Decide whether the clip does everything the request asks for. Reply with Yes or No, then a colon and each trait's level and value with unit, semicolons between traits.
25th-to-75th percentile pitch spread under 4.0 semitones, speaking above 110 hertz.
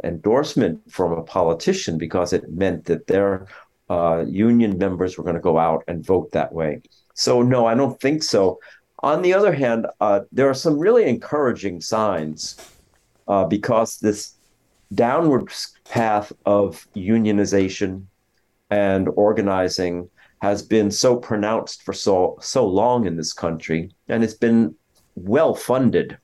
No: average, 3.6 semitones; low, 105 Hz